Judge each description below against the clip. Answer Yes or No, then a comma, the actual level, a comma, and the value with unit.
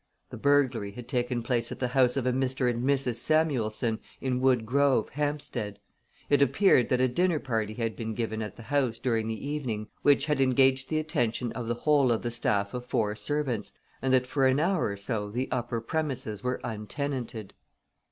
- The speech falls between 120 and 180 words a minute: No, average, 195 wpm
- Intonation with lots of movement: No, average, 3.4 semitones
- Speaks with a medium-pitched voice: No, low, 125 Hz